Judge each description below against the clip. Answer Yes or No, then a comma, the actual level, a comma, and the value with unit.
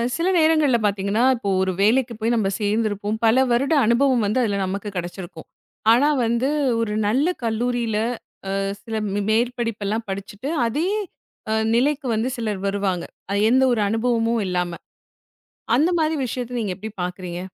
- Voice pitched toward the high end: Yes, high, 225 Hz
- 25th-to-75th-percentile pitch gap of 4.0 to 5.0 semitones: No, average, 3.5 semitones